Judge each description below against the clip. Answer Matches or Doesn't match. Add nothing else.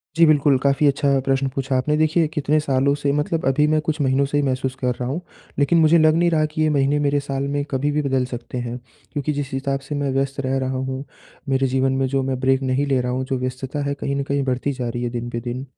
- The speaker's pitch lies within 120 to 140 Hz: Matches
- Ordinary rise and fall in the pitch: Doesn't match